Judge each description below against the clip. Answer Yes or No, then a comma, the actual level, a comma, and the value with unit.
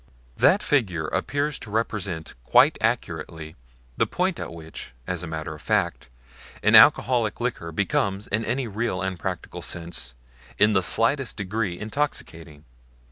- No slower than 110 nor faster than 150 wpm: Yes, average, 140 wpm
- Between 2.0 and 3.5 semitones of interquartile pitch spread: No, wide, 5.6 semitones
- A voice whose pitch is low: Yes, low, 100 Hz